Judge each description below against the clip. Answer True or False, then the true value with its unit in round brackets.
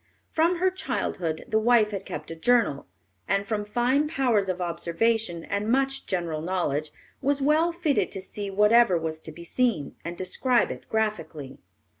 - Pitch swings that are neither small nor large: False (6.5 semitones)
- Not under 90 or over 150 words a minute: False (165 wpm)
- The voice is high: True (210 Hz)